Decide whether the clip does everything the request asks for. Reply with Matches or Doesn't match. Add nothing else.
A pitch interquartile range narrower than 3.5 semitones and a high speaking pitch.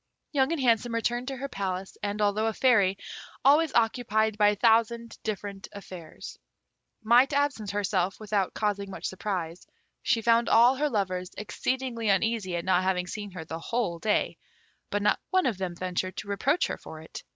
Doesn't match